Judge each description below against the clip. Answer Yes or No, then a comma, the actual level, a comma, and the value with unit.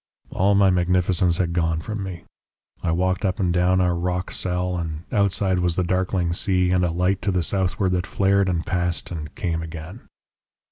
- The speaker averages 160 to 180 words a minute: No, average, 190 wpm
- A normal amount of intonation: No, narrow, 1.4 semitones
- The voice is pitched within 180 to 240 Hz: No, very low, 90 Hz